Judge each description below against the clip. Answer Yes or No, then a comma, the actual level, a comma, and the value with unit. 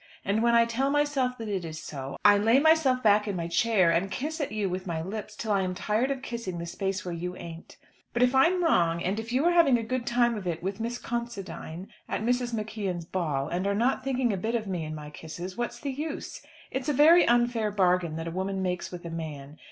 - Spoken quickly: Yes, fast, 250 wpm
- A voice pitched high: Yes, high, 210 Hz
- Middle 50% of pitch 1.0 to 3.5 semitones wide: No, wide, 5.4 semitones